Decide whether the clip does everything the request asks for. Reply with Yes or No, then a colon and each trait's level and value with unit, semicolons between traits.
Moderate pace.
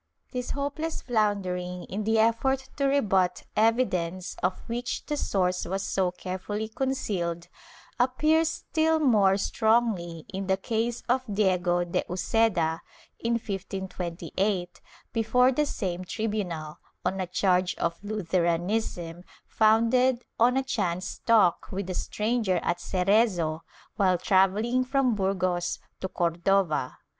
No: slow, 125 wpm